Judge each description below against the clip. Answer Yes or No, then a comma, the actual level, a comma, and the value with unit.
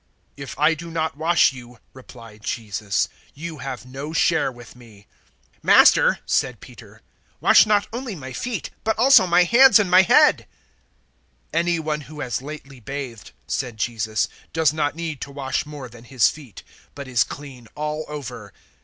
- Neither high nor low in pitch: Yes, medium, 145 Hz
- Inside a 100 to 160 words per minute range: No, average, 170 wpm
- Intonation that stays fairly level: No, average, 4.8 semitones